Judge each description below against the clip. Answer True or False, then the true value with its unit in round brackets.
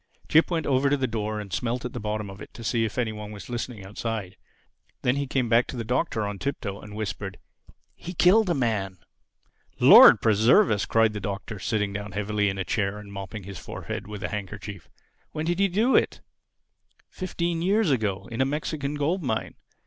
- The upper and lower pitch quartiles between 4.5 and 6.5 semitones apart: True (5.3 semitones)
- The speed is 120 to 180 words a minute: False (200 wpm)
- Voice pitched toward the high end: False (110 Hz)